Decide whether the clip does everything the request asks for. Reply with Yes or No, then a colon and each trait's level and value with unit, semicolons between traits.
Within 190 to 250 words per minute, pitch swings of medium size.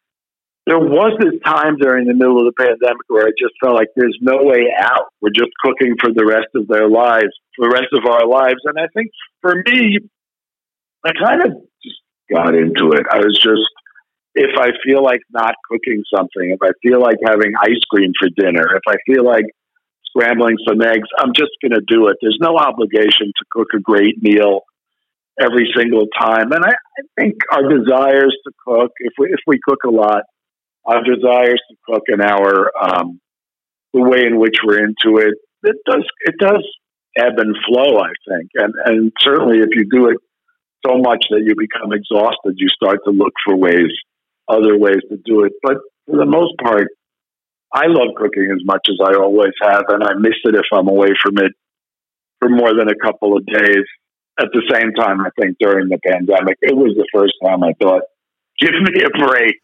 Yes: average, 200 wpm; average, 3.5 semitones